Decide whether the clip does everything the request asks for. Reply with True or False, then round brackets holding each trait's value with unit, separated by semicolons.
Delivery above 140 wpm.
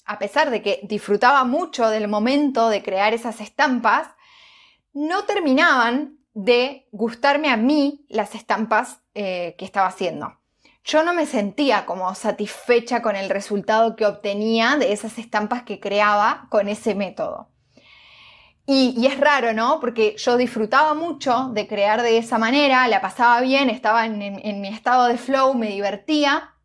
True (160 wpm)